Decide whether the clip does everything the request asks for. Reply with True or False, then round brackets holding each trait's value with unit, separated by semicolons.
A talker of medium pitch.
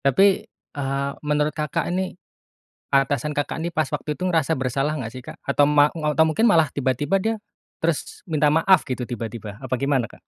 True (150 Hz)